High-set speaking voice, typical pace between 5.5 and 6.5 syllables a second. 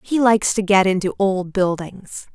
No: high, 195 Hz; 4.6 syllables/s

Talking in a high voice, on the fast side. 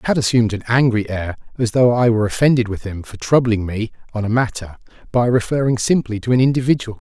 No: low, 115 Hz; fast, 210 wpm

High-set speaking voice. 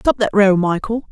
Yes: high, 210 Hz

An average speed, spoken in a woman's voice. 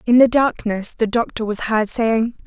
Yes: average, 195 wpm; female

